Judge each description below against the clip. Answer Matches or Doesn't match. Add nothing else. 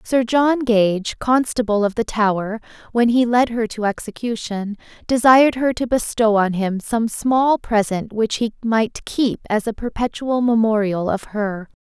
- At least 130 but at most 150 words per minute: Doesn't match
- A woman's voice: Matches